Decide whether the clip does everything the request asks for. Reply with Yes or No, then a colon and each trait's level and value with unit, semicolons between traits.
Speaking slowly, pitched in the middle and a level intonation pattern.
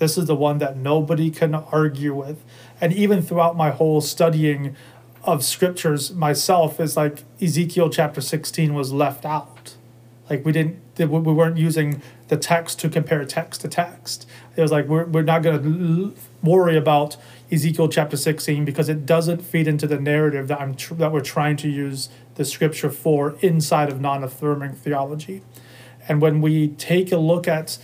No: average, 175 wpm; medium, 155 Hz; narrow, 2.3 semitones